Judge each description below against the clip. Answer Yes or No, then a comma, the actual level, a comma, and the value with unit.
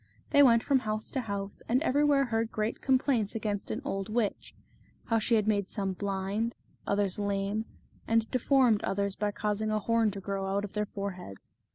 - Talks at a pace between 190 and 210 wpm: Yes, average, 195 wpm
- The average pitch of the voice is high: Yes, high, 215 Hz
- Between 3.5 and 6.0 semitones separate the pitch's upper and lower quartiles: No, narrow, 2.5 semitones